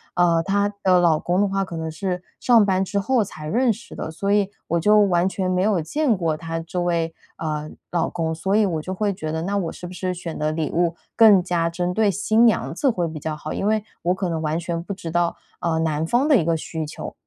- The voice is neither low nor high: Yes, medium, 180 Hz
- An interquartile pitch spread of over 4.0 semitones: No, average, 3.5 semitones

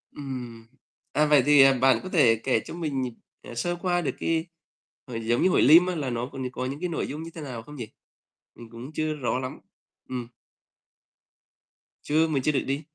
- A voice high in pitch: No, low, 135 Hz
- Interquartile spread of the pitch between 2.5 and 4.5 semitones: Yes, average, 4.1 semitones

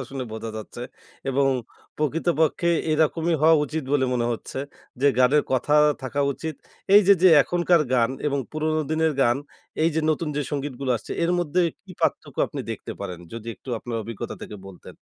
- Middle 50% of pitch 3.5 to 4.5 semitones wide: Yes, average, 4.2 semitones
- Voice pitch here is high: No, medium, 145 Hz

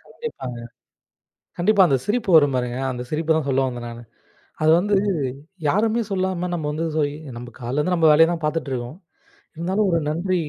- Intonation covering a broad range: Yes, wide, 5.9 semitones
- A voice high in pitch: No, medium, 160 Hz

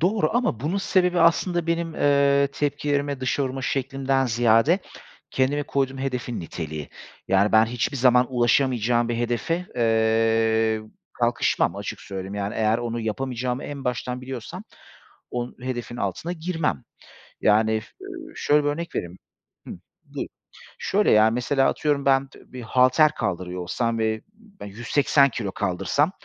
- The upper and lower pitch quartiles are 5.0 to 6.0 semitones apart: No, average, 4.3 semitones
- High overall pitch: No, low, 125 Hz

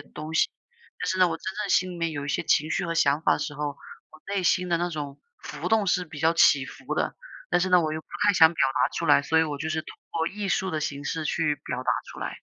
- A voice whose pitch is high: No, medium, 160 Hz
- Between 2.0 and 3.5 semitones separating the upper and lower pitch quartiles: Yes, average, 2.9 semitones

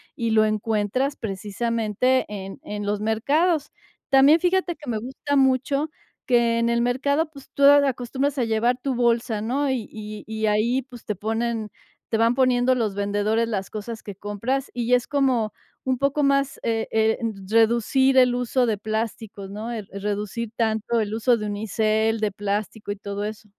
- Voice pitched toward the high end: Yes, high, 230 Hz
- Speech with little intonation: No, average, 3.4 semitones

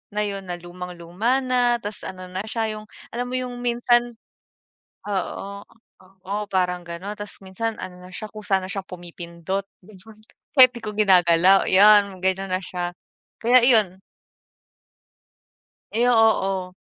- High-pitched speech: Yes, high, 200 Hz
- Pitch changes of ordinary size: Yes, average, 3.4 semitones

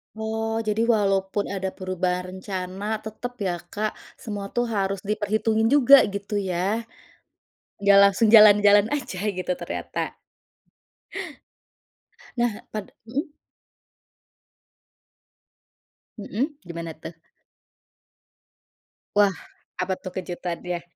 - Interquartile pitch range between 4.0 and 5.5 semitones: No, average, 2.9 semitones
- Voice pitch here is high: Yes, high, 205 Hz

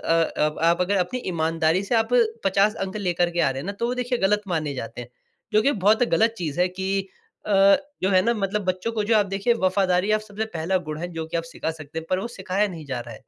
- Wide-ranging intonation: No, average, 4.2 semitones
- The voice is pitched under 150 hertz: No, medium, 185 Hz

